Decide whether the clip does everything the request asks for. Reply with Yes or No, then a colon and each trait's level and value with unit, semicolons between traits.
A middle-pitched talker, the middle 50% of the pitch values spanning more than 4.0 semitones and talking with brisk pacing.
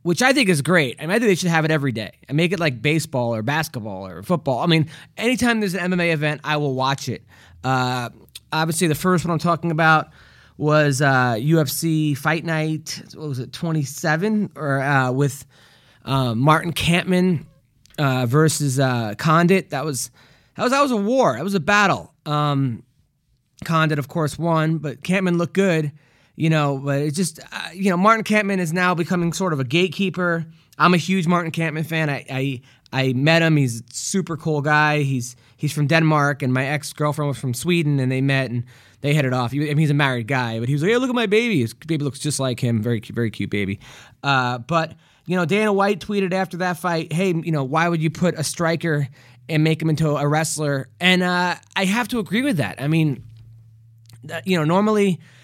Yes: medium, 155 Hz; average, 4.6 semitones; fast, 215 wpm